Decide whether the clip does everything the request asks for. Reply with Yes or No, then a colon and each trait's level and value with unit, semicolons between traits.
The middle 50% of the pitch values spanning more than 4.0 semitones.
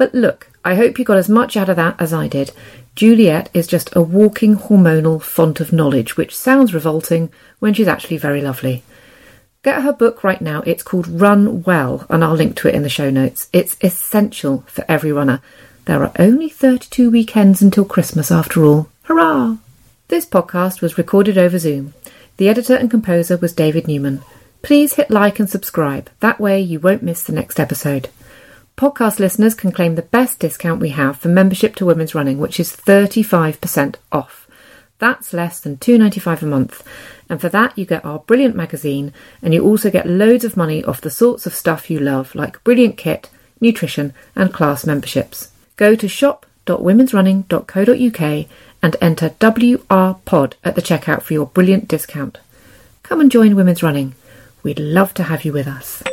Yes: average, 5.3 semitones